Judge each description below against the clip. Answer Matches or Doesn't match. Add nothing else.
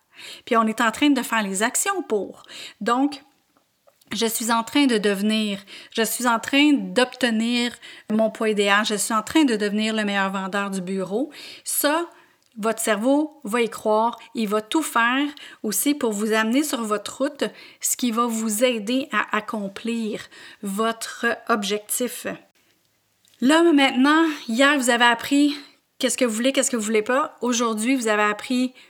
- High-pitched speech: Matches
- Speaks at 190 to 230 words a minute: Doesn't match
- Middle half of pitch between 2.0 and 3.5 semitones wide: Doesn't match